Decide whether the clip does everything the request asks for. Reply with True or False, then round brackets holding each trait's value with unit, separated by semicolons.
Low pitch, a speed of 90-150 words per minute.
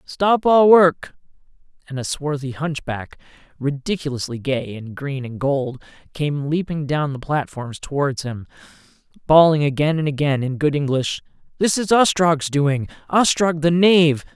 False (150 Hz; 140 wpm)